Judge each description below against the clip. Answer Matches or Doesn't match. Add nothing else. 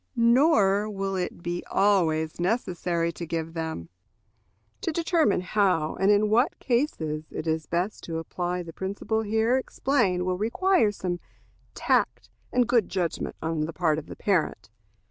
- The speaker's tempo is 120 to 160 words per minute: Matches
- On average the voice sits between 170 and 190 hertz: Matches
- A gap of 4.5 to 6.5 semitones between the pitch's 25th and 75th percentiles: Matches